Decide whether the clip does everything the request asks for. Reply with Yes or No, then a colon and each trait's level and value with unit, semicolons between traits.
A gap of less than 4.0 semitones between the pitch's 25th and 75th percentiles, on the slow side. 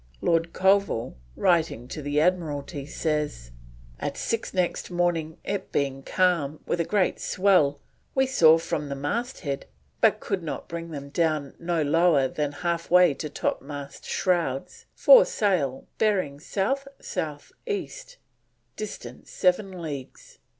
No: average, 4.3 semitones; slow, 130 wpm